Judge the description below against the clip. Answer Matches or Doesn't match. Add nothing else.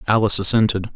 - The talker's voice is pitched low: Matches